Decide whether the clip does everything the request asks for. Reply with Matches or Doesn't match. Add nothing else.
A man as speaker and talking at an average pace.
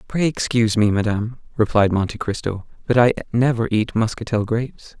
Matches